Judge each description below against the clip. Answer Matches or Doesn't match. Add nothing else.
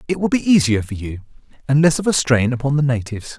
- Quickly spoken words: Matches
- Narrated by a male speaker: Matches